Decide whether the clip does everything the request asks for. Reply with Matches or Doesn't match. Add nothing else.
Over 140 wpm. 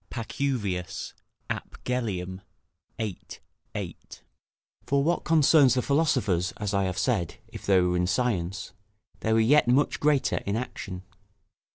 Doesn't match